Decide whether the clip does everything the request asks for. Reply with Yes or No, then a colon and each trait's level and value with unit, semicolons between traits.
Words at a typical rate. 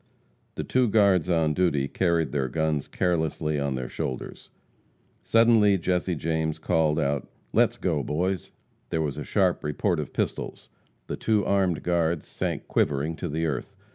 Yes: average, 155 wpm